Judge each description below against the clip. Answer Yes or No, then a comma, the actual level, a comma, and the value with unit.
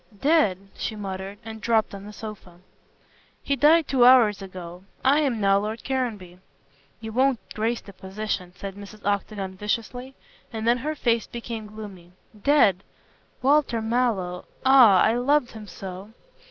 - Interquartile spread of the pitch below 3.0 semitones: No, average, 4.0 semitones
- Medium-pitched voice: No, high, 220 Hz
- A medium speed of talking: Yes, average, 155 wpm